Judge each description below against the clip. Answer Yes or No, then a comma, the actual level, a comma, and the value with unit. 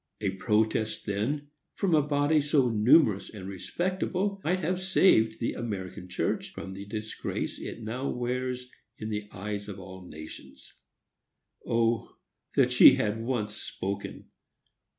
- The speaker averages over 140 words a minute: No, slow, 135 wpm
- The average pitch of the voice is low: Yes, low, 115 Hz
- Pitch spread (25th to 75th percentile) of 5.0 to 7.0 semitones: Yes, wide, 5.5 semitones